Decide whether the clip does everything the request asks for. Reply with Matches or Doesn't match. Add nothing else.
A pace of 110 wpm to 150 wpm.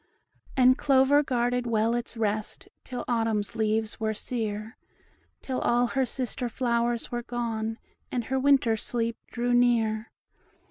Matches